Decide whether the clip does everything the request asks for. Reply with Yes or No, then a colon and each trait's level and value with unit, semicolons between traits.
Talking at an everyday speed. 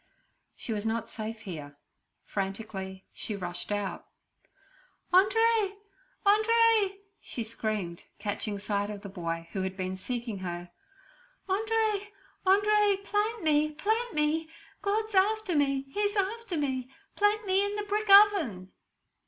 No: slow, 130 wpm